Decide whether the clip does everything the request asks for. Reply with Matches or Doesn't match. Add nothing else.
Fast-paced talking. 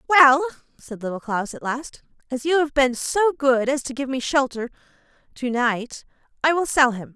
Doesn't match